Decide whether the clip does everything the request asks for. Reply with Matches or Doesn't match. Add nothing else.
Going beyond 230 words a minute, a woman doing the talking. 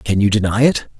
Doesn't match